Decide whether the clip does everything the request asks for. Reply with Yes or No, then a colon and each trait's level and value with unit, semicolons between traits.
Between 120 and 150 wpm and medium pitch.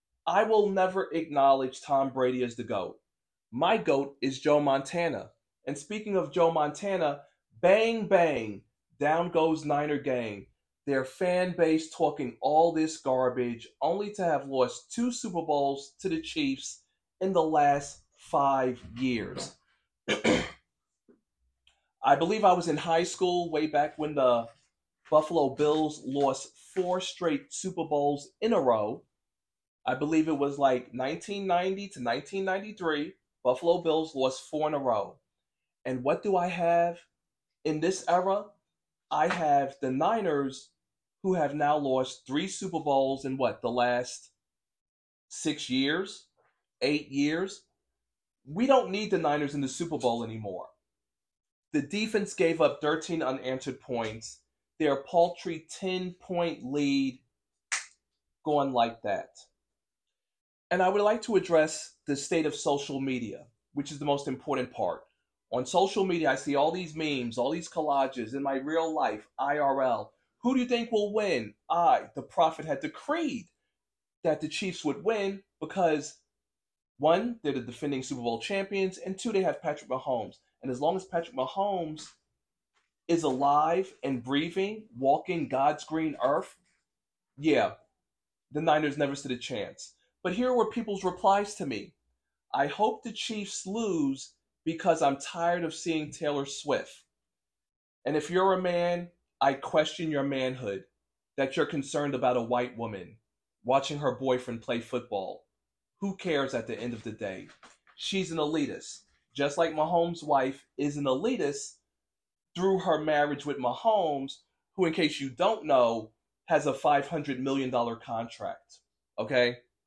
Yes: average, 145 wpm; medium, 150 Hz